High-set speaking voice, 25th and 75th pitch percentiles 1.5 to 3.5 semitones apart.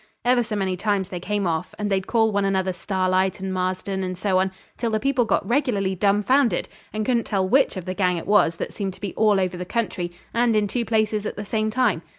Yes: high, 200 Hz; average, 2.8 semitones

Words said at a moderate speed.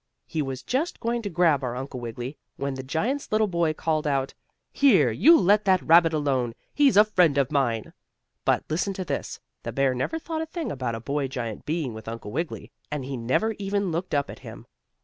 No: fast, 210 wpm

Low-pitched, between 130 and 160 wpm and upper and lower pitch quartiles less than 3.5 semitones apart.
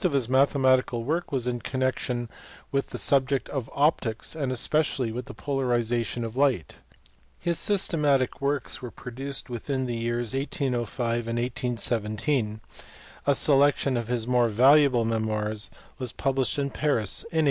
Yes: low, 130 Hz; average, 140 wpm; average, 2.9 semitones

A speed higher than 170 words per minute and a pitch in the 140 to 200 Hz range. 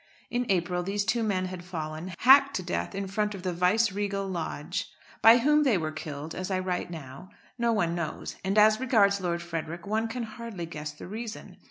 Yes: average, 200 wpm; high, 190 Hz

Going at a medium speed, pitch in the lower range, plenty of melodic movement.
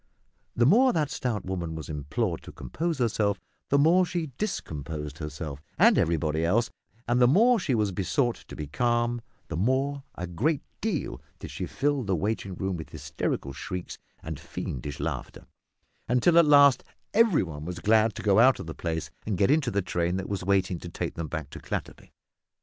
Yes: average, 190 wpm; low, 105 Hz; wide, 8.7 semitones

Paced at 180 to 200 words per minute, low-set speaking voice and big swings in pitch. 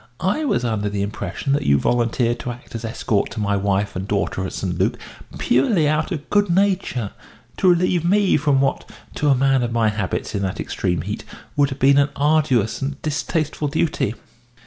Yes: average, 195 wpm; low, 130 Hz; wide, 6.6 semitones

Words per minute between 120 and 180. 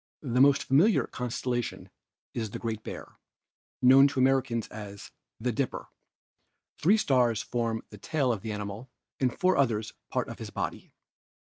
Yes: average, 150 wpm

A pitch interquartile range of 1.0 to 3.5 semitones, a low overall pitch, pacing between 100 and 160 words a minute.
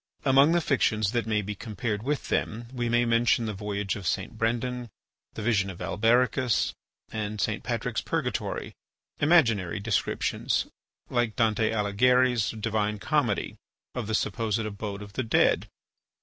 Yes: average, 2.7 semitones; low, 110 Hz; average, 145 wpm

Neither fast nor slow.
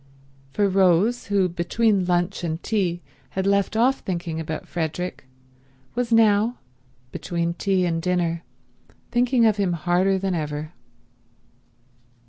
No: slow, 120 wpm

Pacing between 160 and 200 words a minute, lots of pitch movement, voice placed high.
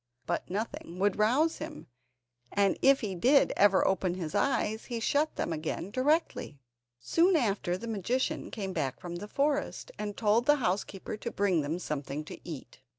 Yes: average, 170 wpm; wide, 6.4 semitones; high, 205 Hz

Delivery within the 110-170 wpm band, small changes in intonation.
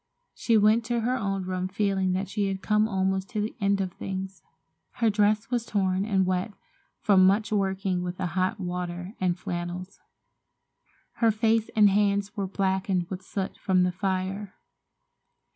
Yes: average, 165 wpm; narrow, 2.0 semitones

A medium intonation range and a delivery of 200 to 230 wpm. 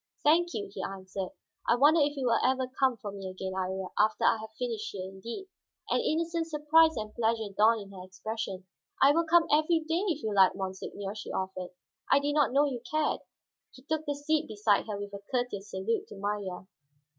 No: wide, 7.0 semitones; fast, 205 wpm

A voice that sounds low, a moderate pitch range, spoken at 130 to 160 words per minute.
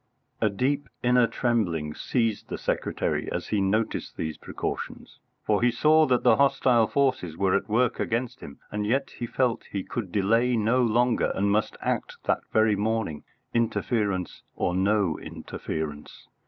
Yes: low, 110 Hz; average, 3.7 semitones; average, 155 wpm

